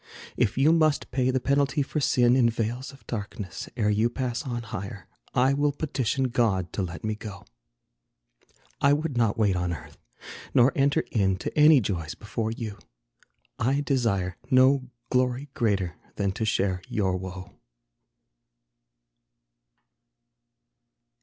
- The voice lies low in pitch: Yes, low, 120 Hz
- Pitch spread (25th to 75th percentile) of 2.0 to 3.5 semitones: No, average, 5.0 semitones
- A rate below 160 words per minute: Yes, average, 140 wpm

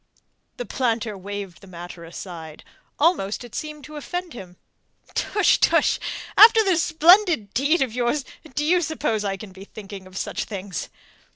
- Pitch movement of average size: No, wide, 8.5 semitones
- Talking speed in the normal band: Yes, average, 160 wpm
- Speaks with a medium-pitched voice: No, high, 235 Hz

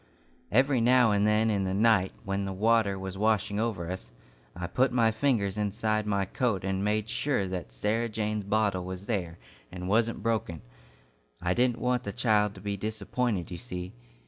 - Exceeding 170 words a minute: Yes, average, 180 wpm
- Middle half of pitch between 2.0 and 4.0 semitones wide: Yes, average, 2.9 semitones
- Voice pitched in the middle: No, low, 105 Hz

